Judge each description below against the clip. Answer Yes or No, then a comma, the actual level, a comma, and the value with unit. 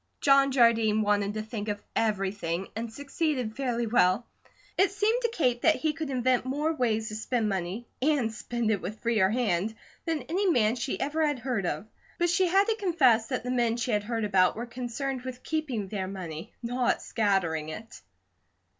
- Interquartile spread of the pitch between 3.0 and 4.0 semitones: No, average, 4.6 semitones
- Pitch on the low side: No, high, 235 Hz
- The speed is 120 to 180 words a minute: No, average, 190 wpm